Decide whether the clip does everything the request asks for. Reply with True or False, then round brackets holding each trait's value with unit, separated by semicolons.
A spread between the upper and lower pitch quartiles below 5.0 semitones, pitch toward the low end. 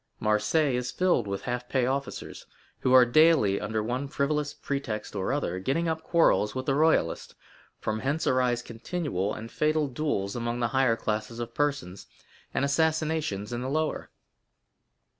False (5.3 semitones; 130 Hz)